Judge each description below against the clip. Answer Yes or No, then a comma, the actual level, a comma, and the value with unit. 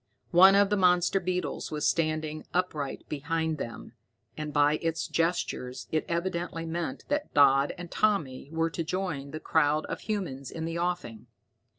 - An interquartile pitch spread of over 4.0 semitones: No, average, 3.2 semitones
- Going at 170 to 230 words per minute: No, average, 160 wpm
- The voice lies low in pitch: No, medium, 165 Hz